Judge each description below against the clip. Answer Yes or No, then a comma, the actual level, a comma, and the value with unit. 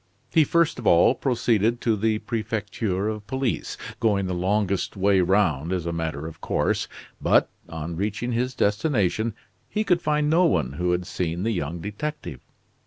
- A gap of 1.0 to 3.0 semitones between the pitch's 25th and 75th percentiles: No, average, 5.1 semitones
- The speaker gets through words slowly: No, average, 170 wpm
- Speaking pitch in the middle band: No, low, 105 Hz